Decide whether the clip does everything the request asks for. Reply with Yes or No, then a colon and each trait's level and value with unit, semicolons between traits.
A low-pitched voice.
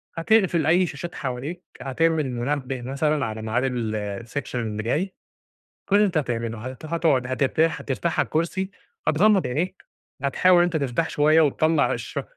No: medium, 145 Hz